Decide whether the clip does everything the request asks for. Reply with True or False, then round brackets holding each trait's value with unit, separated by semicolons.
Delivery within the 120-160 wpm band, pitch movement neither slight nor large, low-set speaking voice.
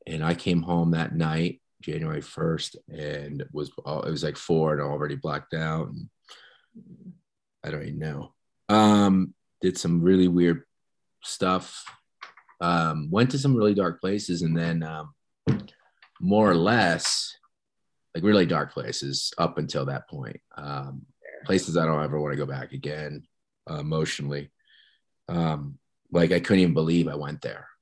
True (155 wpm; 3.3 semitones; 80 Hz)